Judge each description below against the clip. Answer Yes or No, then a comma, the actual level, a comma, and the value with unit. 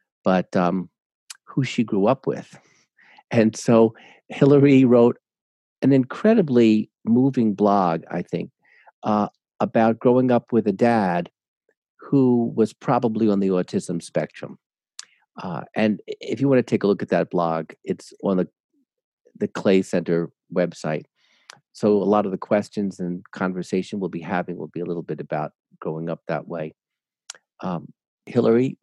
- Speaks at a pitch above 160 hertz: No, low, 110 Hz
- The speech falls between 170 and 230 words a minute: No, average, 150 wpm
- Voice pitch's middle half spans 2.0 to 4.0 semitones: No, average, 4.7 semitones